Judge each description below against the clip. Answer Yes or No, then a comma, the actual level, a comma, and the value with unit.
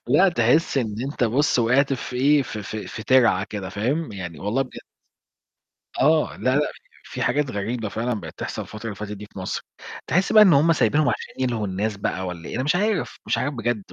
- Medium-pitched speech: No, low, 120 Hz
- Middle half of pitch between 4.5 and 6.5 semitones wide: Yes, wide, 5.5 semitones